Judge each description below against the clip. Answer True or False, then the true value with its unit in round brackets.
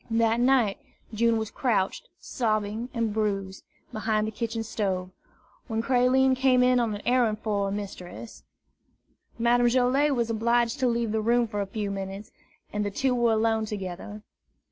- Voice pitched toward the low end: False (225 Hz)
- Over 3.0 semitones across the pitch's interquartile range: False (2.6 semitones)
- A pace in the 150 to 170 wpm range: True (165 wpm)